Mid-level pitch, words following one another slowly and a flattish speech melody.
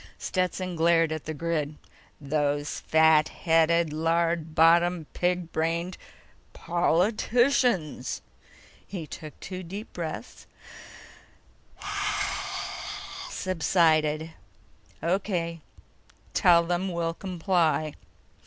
Yes: medium, 170 Hz; slow, 80 wpm; narrow, 2.1 semitones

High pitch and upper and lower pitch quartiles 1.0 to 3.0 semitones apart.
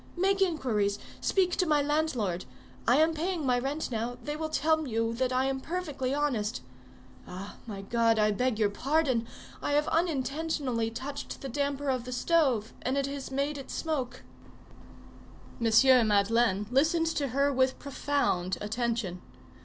No: very high, 265 Hz; average, 4.5 semitones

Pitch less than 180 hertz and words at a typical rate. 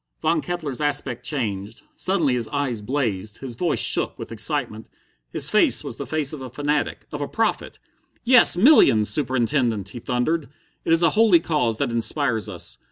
Yes: medium, 140 Hz; average, 170 wpm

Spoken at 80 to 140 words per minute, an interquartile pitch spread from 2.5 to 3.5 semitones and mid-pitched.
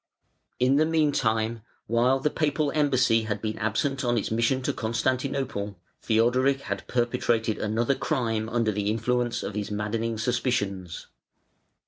No: slow, 135 wpm; average, 2.9 semitones; low, 115 Hz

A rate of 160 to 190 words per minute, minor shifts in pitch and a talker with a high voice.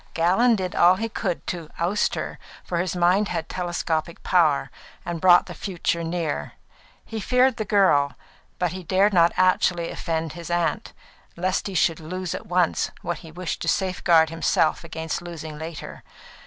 No: average, 170 wpm; narrow, 2.2 semitones; medium, 175 Hz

